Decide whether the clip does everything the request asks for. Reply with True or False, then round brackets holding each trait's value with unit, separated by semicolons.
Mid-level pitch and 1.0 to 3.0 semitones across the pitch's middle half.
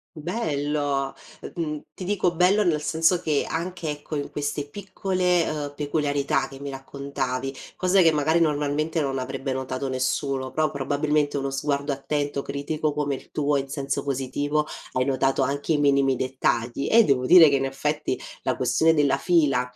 True (145 Hz; 2.4 semitones)